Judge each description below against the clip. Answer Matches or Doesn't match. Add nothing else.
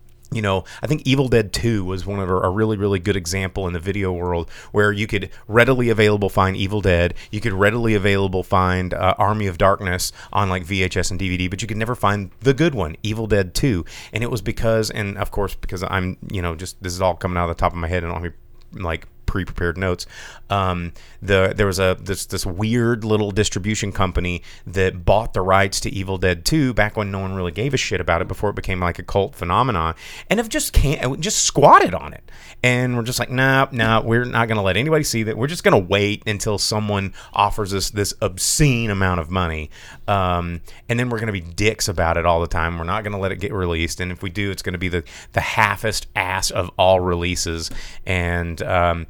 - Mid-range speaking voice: Doesn't match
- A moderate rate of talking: Doesn't match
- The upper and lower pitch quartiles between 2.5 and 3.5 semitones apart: Matches